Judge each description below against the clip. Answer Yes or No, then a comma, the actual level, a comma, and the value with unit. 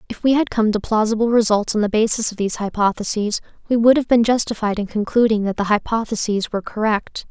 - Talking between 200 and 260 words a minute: Yes, fast, 205 wpm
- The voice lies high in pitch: Yes, high, 215 Hz